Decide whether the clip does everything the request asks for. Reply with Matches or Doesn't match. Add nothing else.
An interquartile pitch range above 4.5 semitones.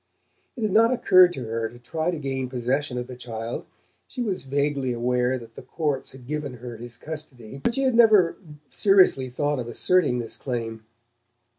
Matches